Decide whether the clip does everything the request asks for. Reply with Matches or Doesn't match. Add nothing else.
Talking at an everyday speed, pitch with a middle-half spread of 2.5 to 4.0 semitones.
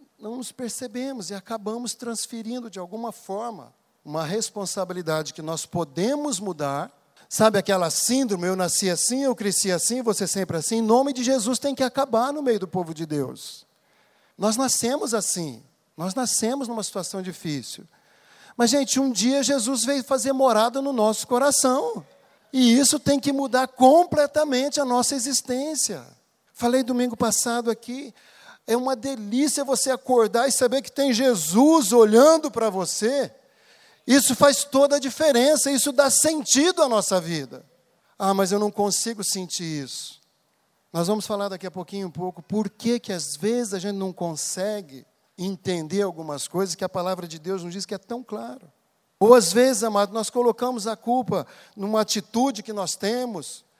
Doesn't match